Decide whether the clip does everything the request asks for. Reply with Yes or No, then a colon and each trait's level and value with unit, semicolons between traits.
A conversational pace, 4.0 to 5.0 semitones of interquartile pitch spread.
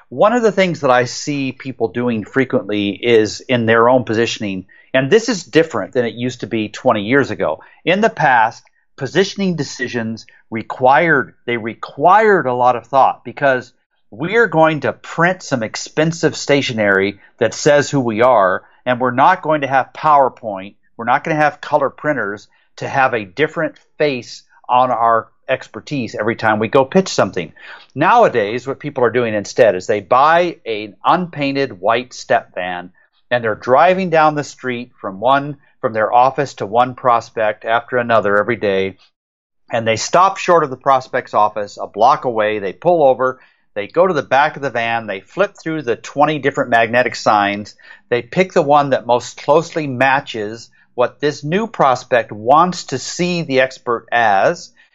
Yes: average, 175 wpm; average, 4.7 semitones